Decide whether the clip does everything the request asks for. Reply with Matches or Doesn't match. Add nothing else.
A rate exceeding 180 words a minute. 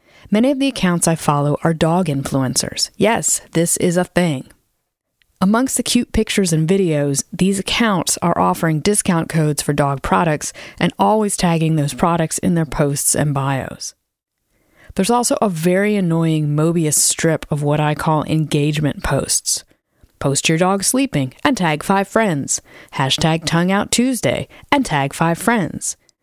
Doesn't match